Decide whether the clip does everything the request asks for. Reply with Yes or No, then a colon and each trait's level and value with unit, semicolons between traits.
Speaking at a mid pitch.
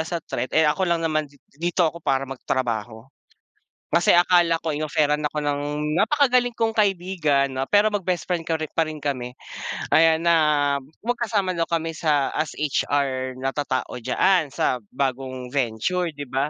Yes: medium, 155 Hz